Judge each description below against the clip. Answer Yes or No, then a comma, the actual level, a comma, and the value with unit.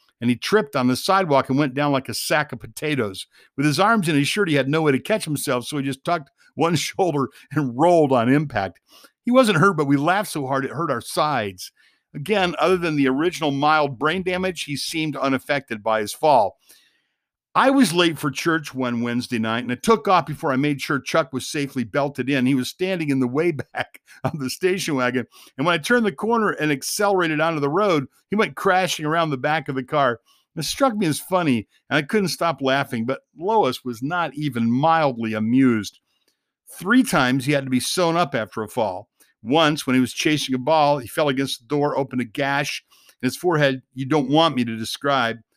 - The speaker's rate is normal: No, fast, 220 wpm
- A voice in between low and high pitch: Yes, medium, 145 Hz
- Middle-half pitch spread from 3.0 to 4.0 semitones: No, average, 4.4 semitones